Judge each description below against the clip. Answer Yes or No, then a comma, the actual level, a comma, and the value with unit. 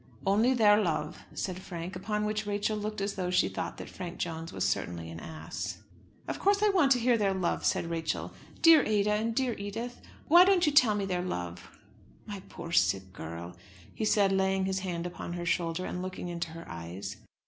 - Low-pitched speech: No, high, 190 Hz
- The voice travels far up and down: No, average, 4.2 semitones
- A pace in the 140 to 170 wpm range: No, fast, 205 wpm